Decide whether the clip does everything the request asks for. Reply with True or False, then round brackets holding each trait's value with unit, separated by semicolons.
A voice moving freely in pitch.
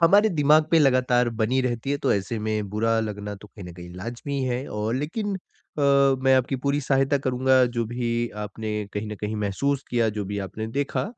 False (4.3 semitones)